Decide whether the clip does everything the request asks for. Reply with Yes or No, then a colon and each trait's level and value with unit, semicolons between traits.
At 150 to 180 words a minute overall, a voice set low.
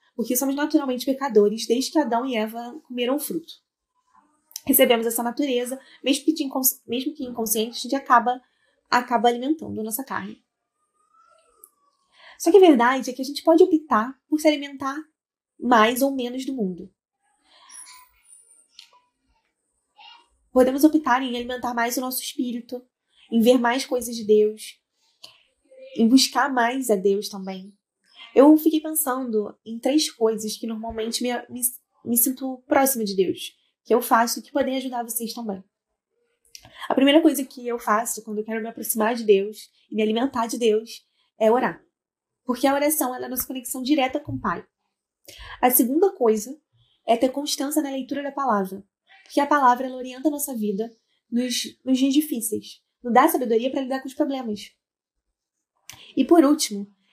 No: average, 160 wpm; very high, 255 Hz